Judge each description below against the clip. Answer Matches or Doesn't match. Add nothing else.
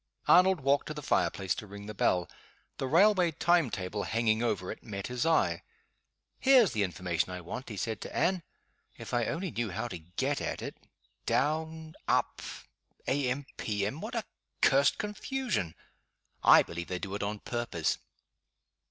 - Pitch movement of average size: Doesn't match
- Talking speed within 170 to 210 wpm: Matches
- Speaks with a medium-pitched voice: Doesn't match